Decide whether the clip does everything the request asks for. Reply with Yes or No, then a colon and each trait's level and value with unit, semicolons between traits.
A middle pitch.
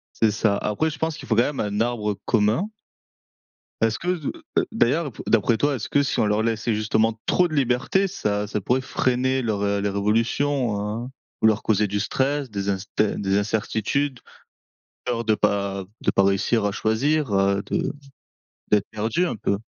No: low, 110 Hz